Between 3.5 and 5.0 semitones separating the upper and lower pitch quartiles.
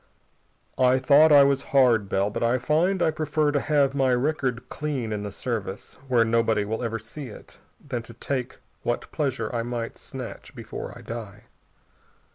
Yes: average, 3.8 semitones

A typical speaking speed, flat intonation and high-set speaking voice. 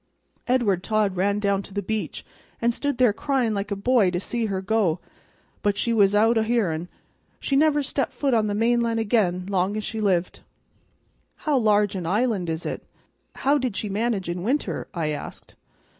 No: average, 190 wpm; average, 3.6 semitones; high, 210 Hz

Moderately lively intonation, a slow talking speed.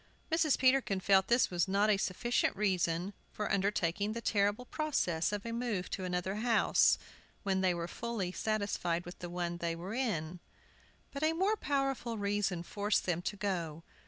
No: average, 4.6 semitones; average, 170 wpm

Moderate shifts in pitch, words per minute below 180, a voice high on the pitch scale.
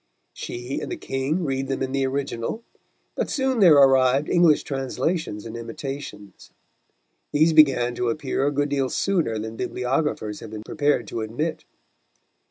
No: average, 4.0 semitones; average, 155 wpm; low, 135 Hz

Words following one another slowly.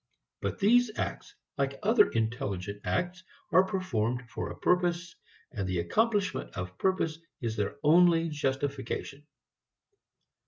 Yes: slow, 120 wpm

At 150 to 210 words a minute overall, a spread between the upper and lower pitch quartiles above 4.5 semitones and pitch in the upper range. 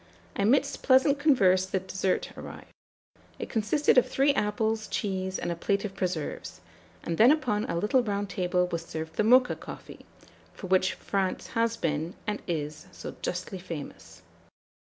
No: average, 155 wpm; average, 4.2 semitones; high, 195 Hz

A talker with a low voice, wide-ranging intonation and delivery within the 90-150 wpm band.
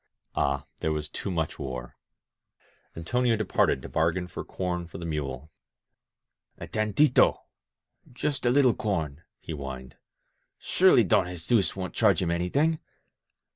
Yes: very low, 90 Hz; wide, 6.1 semitones; slow, 135 wpm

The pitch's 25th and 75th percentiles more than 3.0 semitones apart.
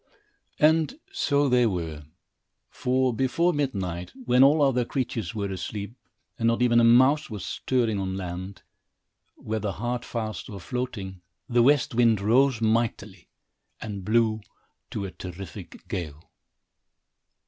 Yes: average, 4.6 semitones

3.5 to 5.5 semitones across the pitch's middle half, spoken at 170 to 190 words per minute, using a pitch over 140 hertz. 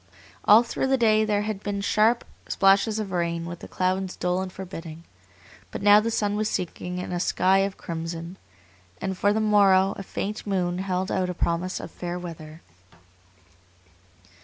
No: narrow, 2.6 semitones; average, 175 wpm; high, 190 Hz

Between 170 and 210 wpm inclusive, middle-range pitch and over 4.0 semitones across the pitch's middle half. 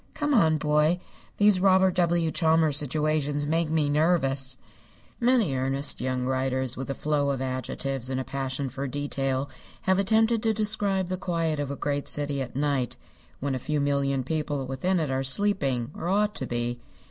Yes: average, 175 wpm; medium, 145 Hz; average, 4.5 semitones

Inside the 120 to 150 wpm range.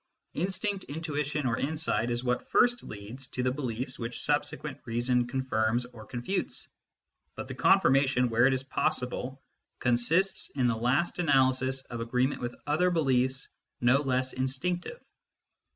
Yes: average, 145 wpm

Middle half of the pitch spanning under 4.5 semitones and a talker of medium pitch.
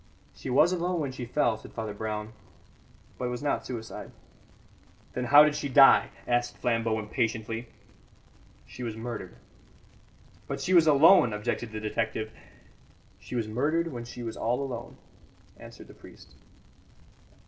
No: average, 4.0 semitones; low, 120 Hz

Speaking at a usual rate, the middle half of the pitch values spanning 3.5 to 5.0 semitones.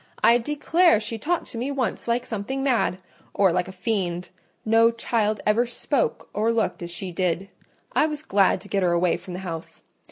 Yes: average, 190 wpm; average, 4.7 semitones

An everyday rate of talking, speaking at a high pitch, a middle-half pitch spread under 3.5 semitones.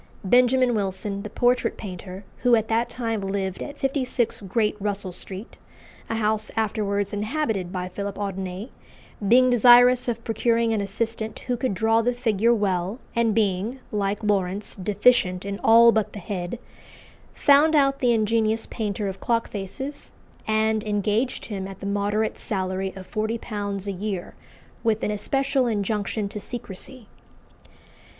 Yes: average, 150 wpm; high, 215 Hz; average, 2.9 semitones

